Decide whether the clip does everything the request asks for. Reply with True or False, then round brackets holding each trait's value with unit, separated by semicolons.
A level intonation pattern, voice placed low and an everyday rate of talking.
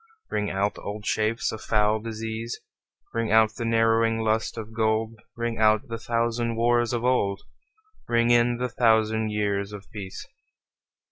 True (1.4 semitones; 110 Hz; 150 wpm)